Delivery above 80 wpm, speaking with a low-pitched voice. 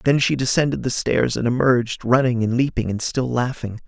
Yes: average, 200 wpm; low, 125 Hz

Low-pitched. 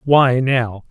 Yes: low, 125 Hz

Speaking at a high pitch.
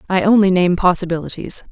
No: medium, 180 Hz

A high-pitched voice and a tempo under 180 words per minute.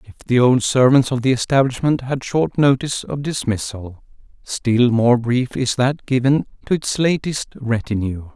No: low, 125 Hz; average, 160 wpm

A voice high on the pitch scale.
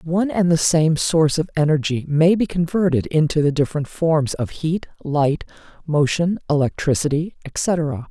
No: medium, 160 Hz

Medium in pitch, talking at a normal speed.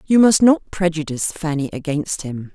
Yes: medium, 165 Hz; average, 165 wpm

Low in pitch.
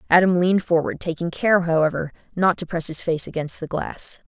No: medium, 170 Hz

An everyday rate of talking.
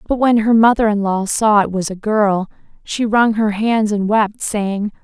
No: fast, 215 wpm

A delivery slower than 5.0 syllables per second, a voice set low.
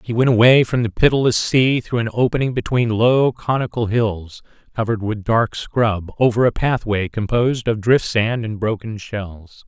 Yes: 4.7 syllables/s; low, 115 Hz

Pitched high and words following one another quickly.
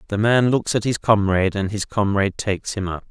No: low, 105 Hz; fast, 230 wpm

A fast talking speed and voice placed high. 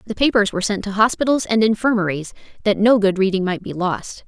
Yes: fast, 210 wpm; high, 205 Hz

